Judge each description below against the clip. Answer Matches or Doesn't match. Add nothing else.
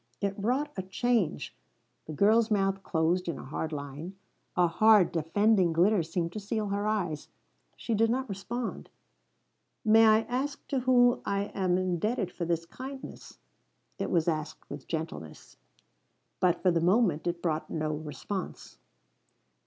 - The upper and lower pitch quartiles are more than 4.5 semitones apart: Matches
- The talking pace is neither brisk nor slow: Matches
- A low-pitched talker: Doesn't match